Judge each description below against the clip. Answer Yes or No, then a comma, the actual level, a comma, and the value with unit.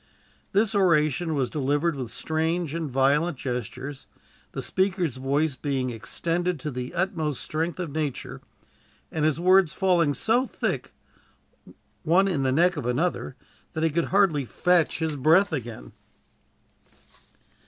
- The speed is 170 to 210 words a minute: No, slow, 135 wpm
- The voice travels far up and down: No, average, 4.3 semitones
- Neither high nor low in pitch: Yes, medium, 155 Hz